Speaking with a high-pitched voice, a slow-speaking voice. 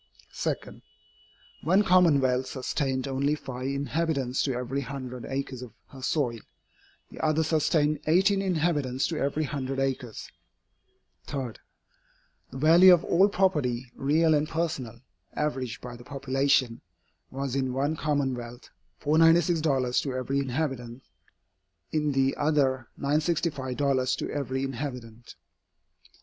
No: medium, 140 Hz; slow, 115 wpm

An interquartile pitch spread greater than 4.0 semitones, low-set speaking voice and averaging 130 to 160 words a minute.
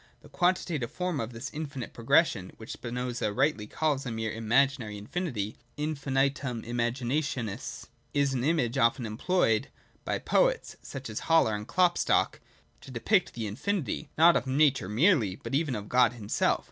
Yes: average, 5.1 semitones; low, 130 Hz; average, 150 wpm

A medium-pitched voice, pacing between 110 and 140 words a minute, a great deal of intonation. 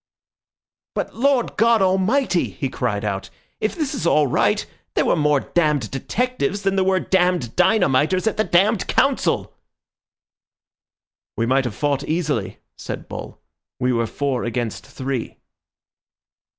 Yes: medium, 155 Hz; slow, 135 wpm; wide, 7.1 semitones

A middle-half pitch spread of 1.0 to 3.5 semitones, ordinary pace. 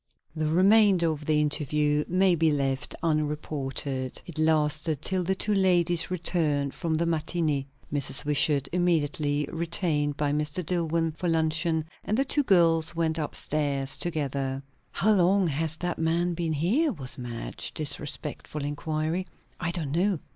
Yes: average, 2.9 semitones; average, 145 wpm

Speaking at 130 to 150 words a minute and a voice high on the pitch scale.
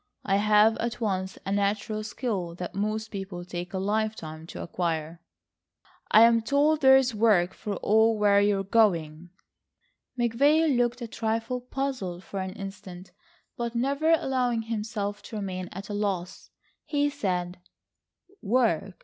Yes: average, 140 wpm; high, 210 Hz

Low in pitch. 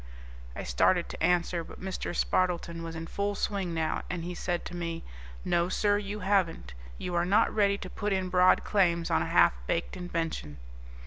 No: medium, 180 Hz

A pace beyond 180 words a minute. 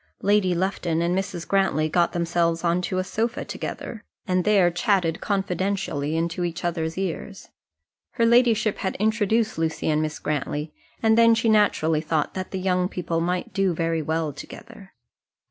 No: average, 165 wpm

